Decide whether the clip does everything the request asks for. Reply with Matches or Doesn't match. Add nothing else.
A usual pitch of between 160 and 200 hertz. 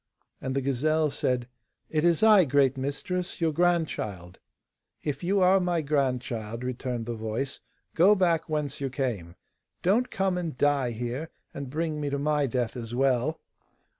Doesn't match